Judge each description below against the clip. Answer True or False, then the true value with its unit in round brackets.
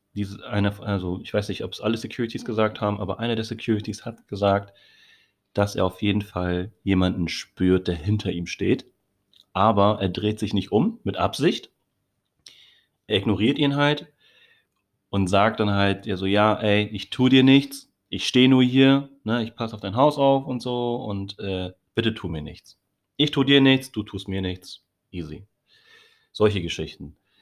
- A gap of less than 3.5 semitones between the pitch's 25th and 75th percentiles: False (3.8 semitones)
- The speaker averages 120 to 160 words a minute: False (175 wpm)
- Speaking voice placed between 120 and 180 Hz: False (105 Hz)